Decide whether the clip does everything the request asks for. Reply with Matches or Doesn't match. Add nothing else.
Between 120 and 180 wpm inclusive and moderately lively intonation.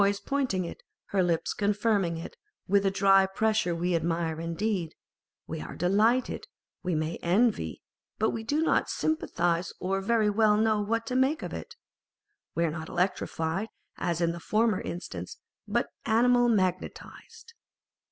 Matches